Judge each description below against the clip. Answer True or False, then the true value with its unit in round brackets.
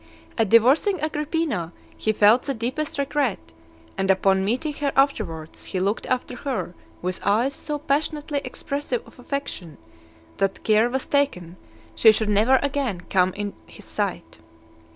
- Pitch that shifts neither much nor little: False (6.3 semitones)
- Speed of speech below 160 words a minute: True (150 wpm)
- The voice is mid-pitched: False (245 Hz)